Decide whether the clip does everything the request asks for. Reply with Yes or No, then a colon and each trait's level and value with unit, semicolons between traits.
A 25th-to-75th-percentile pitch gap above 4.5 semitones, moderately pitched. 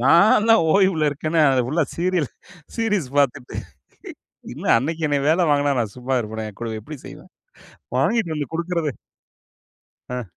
Yes: average, 4.9 semitones; medium, 155 Hz